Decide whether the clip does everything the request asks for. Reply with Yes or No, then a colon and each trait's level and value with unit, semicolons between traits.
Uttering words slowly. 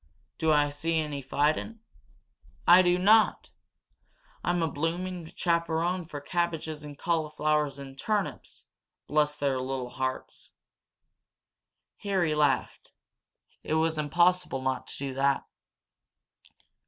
Yes: slow, 110 wpm